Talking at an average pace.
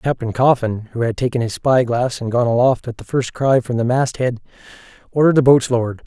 No: fast, 220 wpm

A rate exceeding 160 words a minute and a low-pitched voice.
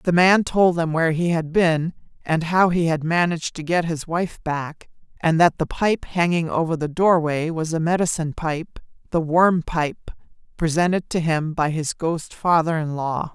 No: average, 180 wpm; medium, 165 Hz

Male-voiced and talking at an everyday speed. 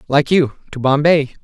Yes: male; average, 170 wpm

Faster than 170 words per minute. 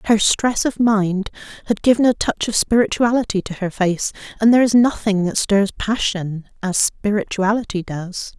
No: average, 165 wpm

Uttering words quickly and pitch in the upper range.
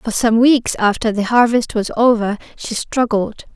No: average, 170 wpm; high, 225 Hz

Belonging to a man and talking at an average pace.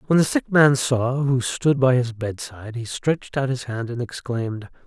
No: male; fast, 210 wpm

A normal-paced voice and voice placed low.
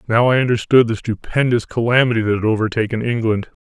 Yes: average, 165 wpm; low, 115 Hz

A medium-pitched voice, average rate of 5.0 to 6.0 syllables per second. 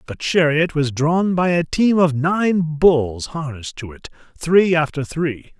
No: medium, 160 Hz; 4.0 syllables/s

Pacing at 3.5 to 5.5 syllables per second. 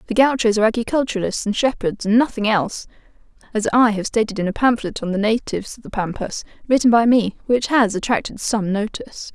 No: 6.0 syllables/s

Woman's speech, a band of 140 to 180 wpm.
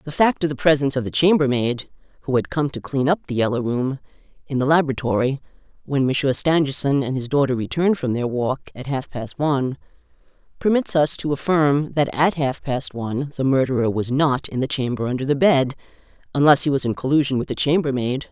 No: female; average, 195 wpm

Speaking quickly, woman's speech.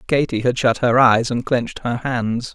No: fast, 210 wpm; male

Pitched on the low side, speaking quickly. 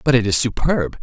Yes: low, 125 Hz; fast, 235 wpm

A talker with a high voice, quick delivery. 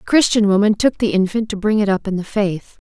Yes: high, 205 Hz; fast, 270 wpm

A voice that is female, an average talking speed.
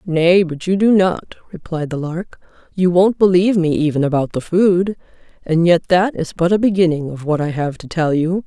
No: female; fast, 215 wpm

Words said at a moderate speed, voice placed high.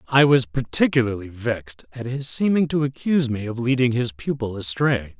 No: average, 175 wpm; low, 125 Hz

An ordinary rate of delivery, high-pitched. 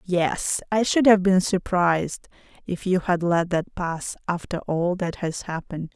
No: average, 170 wpm; medium, 180 Hz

